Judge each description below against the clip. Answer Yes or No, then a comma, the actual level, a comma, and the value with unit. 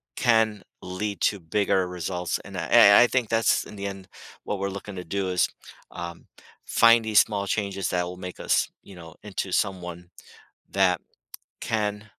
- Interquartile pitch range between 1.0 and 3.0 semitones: Yes, narrow, 2.6 semitones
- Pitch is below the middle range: Yes, low, 100 Hz